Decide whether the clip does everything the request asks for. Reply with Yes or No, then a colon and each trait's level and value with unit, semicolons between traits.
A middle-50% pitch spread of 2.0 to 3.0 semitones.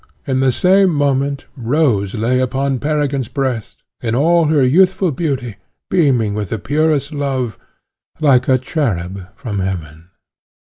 No: average, 4.7 semitones